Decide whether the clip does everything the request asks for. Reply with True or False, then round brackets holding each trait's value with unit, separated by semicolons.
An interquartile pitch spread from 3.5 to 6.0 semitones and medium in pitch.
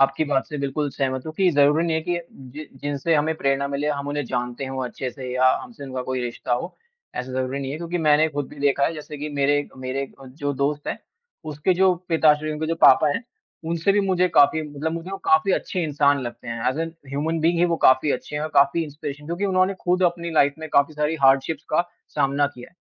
False (2.8 semitones; 145 Hz)